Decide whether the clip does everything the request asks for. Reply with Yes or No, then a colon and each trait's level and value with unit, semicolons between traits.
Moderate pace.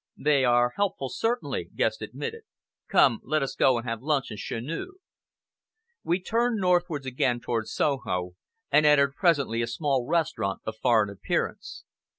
Yes: average, 150 wpm